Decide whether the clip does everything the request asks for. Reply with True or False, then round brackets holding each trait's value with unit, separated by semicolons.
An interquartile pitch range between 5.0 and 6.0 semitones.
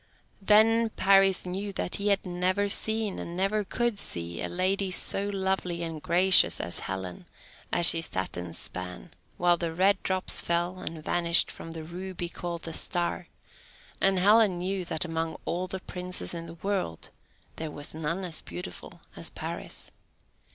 False (2.9 semitones)